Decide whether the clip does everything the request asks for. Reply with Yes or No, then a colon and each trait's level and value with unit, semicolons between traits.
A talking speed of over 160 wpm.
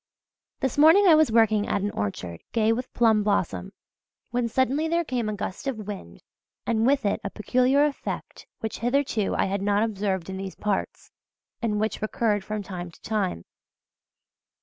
Yes: average, 170 wpm